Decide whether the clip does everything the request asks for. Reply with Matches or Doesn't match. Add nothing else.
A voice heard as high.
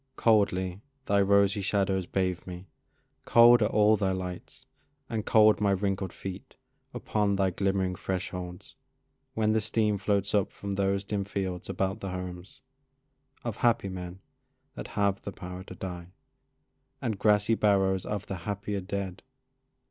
Doesn't match